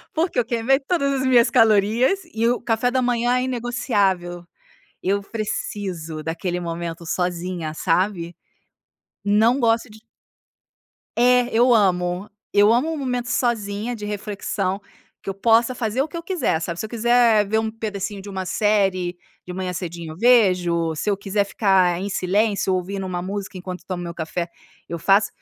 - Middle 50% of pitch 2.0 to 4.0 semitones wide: No, average, 4.6 semitones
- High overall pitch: Yes, high, 205 Hz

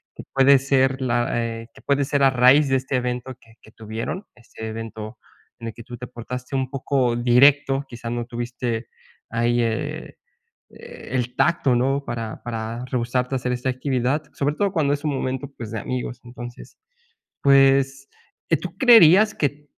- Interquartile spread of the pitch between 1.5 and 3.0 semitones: Yes, average, 2.7 semitones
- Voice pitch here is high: No, low, 125 Hz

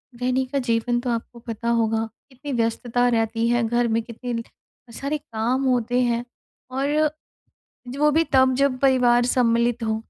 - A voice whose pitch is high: Yes, high, 240 Hz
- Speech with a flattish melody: Yes, narrow, 2.0 semitones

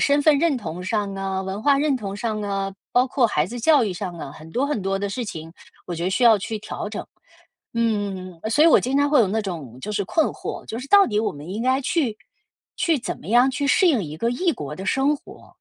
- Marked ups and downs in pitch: Yes, wide, 5.8 semitones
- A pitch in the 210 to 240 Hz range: Yes, high, 215 Hz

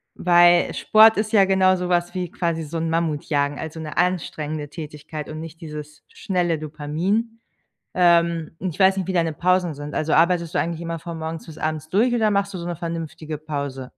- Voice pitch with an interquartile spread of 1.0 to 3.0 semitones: Yes, average, 2.7 semitones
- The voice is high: No, medium, 165 Hz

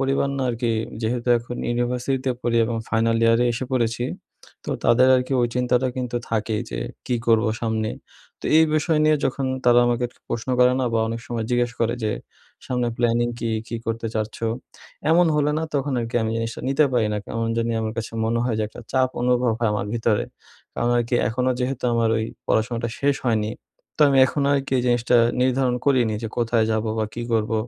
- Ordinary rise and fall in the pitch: No, narrow, 1.9 semitones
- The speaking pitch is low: Yes, low, 120 Hz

